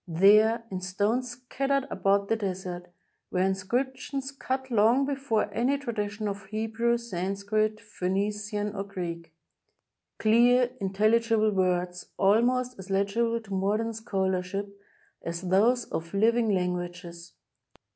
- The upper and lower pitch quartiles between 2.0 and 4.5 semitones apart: Yes, average, 3.7 semitones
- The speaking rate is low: Yes, slow, 125 wpm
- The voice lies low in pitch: No, high, 210 Hz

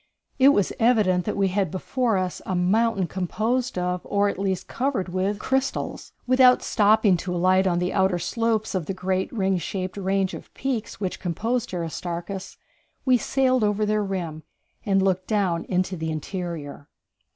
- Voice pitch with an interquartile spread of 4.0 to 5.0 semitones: No, average, 3.2 semitones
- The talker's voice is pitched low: No, high, 190 Hz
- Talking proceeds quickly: No, average, 165 wpm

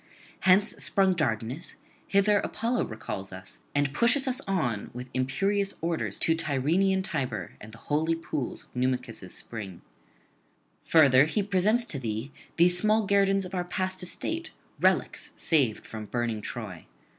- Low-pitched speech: No, medium, 160 Hz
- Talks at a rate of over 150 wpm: No, average, 145 wpm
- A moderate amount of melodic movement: No, wide, 8.0 semitones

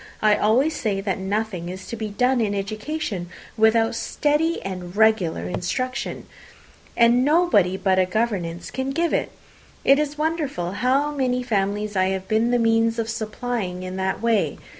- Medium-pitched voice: No, high, 220 Hz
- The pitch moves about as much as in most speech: Yes, average, 4.8 semitones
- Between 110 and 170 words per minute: Yes, average, 160 wpm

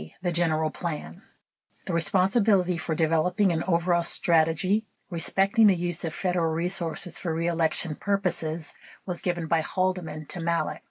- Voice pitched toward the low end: No, medium, 170 Hz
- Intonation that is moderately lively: No, narrow, 2.2 semitones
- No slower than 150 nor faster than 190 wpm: No, average, 140 wpm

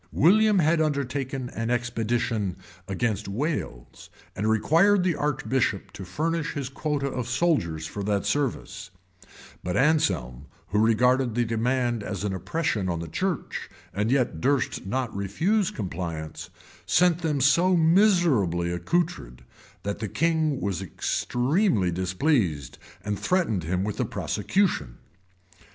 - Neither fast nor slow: No, slow, 130 wpm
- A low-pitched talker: Yes, low, 120 Hz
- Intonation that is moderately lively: No, wide, 8.2 semitones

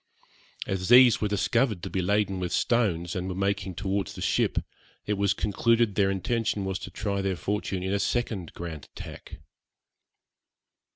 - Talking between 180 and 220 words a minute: No, average, 165 wpm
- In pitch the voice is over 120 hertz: No, low, 100 Hz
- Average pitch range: No, narrow, 1.9 semitones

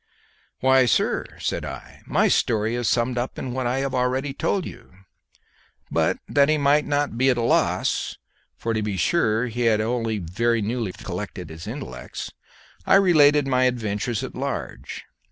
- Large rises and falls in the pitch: No, average, 3.5 semitones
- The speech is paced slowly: No, average, 170 wpm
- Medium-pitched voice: No, low, 120 Hz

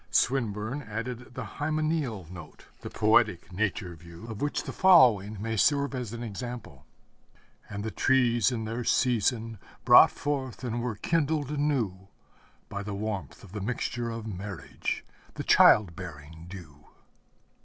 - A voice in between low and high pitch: No, low, 115 Hz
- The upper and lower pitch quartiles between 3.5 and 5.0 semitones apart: Yes, average, 4.3 semitones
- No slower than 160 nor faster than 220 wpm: No, average, 145 wpm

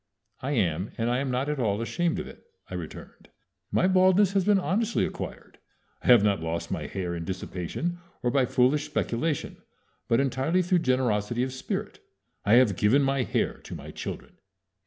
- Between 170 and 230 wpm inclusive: Yes, average, 180 wpm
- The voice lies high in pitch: No, low, 130 Hz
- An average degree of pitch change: No, wide, 7.5 semitones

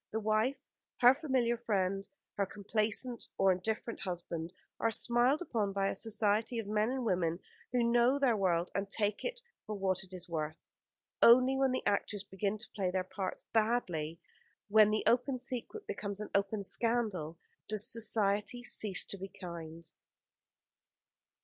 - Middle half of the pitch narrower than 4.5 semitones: Yes, average, 3.8 semitones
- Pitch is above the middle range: Yes, high, 210 Hz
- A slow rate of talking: No, average, 160 wpm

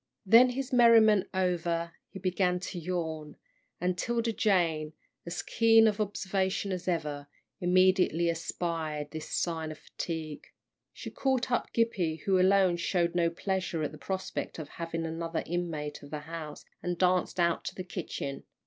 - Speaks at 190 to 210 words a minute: No, average, 155 wpm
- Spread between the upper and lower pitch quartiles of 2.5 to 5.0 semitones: Yes, average, 2.9 semitones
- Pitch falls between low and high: Yes, medium, 175 Hz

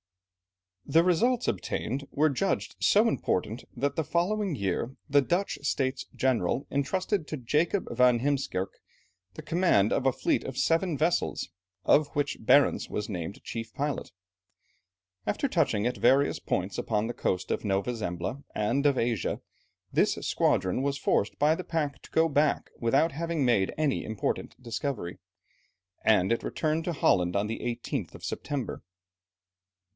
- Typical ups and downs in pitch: No, wide, 5.9 semitones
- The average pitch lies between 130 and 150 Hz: Yes, low, 135 Hz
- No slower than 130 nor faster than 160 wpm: Yes, average, 150 wpm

